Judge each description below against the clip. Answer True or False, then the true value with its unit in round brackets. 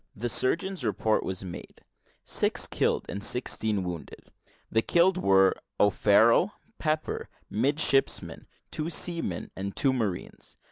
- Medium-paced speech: False (125 wpm)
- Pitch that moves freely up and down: True (7.7 semitones)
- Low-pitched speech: True (115 Hz)